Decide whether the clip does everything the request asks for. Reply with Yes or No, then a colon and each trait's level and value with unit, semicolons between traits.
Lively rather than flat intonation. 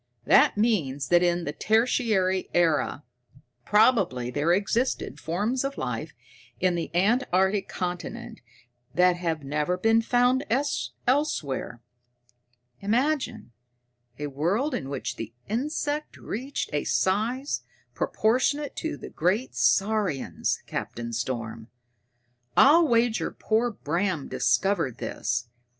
Yes: wide, 8.2 semitones